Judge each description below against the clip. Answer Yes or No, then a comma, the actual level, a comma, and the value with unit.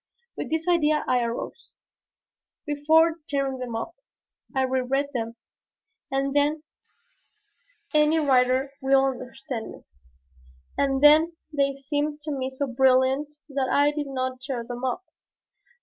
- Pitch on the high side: Yes, very high, 275 Hz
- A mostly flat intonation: Yes, narrow, 2.3 semitones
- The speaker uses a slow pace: Yes, slow, 130 wpm